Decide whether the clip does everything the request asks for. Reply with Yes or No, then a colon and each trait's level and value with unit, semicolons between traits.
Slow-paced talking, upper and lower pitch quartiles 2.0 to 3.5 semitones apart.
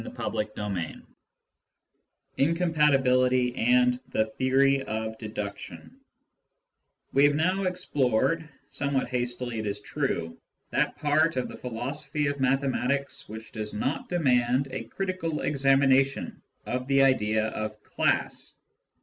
No: slow, 115 wpm; average, 4.2 semitones